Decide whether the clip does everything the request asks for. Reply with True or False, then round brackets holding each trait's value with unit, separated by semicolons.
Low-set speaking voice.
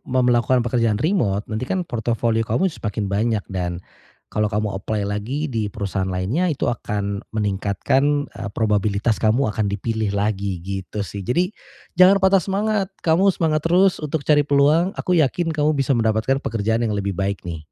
True (115 Hz)